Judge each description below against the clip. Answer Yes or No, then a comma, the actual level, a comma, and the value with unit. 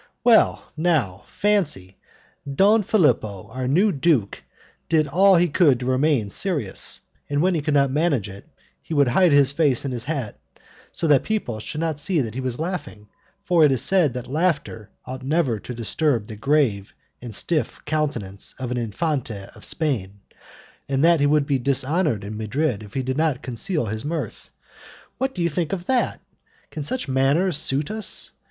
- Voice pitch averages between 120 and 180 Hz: Yes, medium, 140 Hz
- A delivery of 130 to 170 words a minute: No, average, 180 wpm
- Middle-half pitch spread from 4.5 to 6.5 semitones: Yes, wide, 5.5 semitones